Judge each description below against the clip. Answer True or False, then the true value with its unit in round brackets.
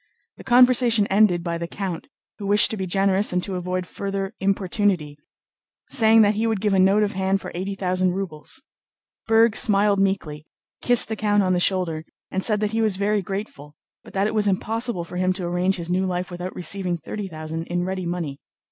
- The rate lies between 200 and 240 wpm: True (205 wpm)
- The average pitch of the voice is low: False (190 Hz)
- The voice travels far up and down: False (2.7 semitones)